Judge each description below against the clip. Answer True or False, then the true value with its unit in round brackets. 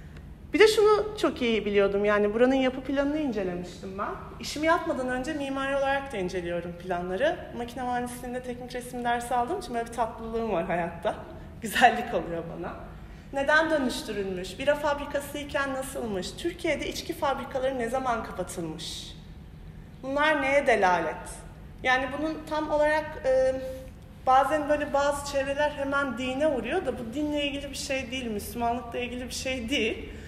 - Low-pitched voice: False (260 Hz)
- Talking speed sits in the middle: False (145 wpm)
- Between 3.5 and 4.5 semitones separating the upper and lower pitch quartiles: True (3.9 semitones)